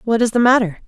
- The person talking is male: No, female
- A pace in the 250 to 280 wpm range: Yes, fast, 275 wpm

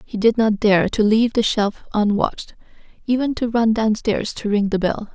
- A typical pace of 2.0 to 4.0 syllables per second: No, 4.9 syllables/s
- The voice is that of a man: No, female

